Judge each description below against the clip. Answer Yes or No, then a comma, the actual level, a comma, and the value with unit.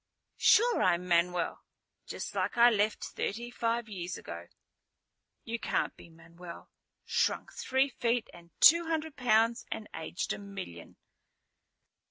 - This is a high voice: Yes, high, 215 Hz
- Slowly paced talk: Yes, slow, 130 wpm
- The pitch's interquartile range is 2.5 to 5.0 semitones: No, wide, 5.6 semitones